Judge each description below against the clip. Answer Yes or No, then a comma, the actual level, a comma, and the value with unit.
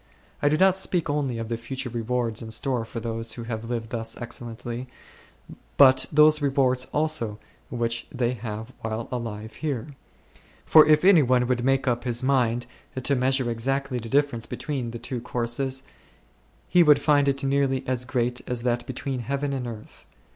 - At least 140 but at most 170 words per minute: No, average, 180 wpm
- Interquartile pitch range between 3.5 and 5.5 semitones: No, average, 2.9 semitones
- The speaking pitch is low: Yes, low, 125 Hz